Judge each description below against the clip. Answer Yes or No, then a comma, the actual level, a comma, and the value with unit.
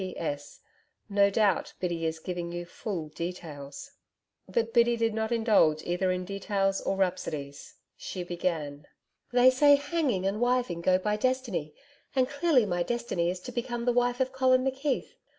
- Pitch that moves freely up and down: Yes, wide, 6.0 semitones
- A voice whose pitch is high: Yes, high, 200 Hz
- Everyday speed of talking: Yes, average, 160 wpm